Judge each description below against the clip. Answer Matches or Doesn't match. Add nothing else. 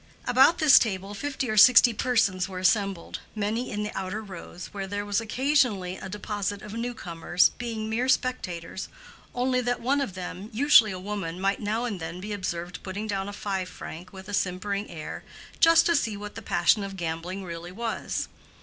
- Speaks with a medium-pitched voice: Doesn't match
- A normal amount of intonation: Matches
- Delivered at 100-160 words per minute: Doesn't match